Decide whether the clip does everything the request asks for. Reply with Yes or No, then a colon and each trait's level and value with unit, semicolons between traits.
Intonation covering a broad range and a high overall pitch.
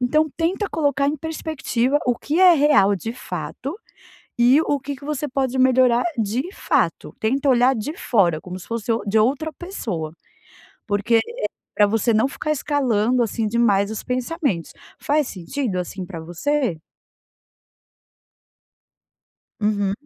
Yes: wide, 5.7 semitones; high, 245 Hz